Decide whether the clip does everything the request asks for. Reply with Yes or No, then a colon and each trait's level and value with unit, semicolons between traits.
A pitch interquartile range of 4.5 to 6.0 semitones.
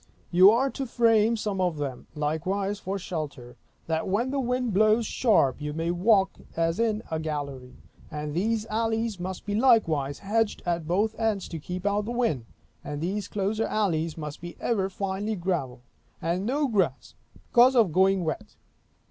Yes: wide, 5.4 semitones